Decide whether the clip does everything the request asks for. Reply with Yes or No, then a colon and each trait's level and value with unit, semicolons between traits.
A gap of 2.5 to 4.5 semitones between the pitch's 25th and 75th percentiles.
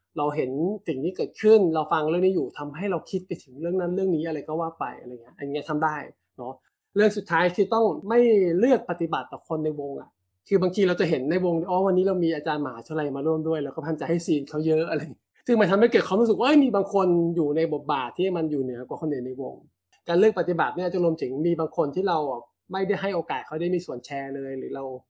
Yes: average, 4.0 semitones